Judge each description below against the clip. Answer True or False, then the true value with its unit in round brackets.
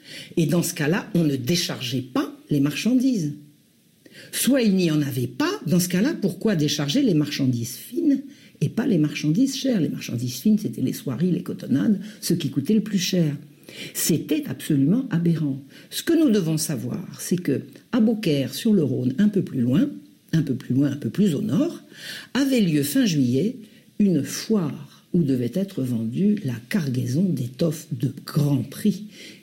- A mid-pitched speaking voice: True (170 Hz)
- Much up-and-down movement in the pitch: True (7.1 semitones)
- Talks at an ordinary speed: True (175 wpm)